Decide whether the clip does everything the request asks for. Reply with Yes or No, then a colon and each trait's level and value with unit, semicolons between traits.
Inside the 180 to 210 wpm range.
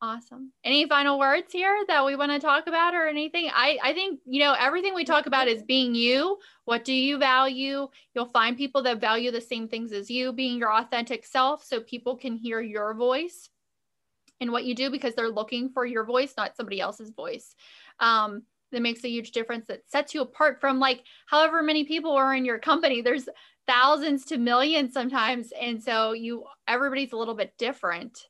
Yes: average, 200 wpm